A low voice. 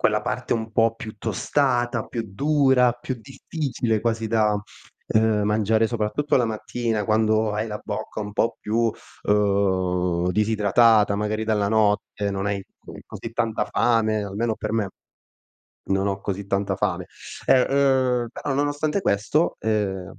Yes: low, 110 Hz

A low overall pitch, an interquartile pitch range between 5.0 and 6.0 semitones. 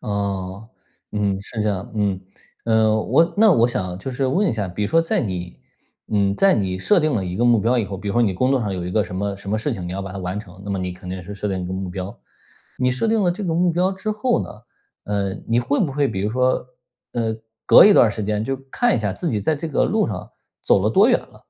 Yes: low, 105 Hz; wide, 5.6 semitones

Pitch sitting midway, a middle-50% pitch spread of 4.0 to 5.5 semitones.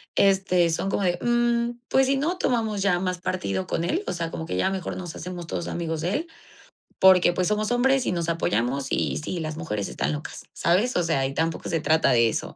Yes: medium, 175 Hz; average, 4.7 semitones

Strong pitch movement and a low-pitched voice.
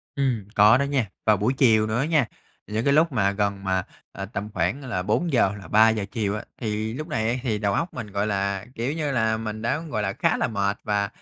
No: average, 4.0 semitones; low, 110 Hz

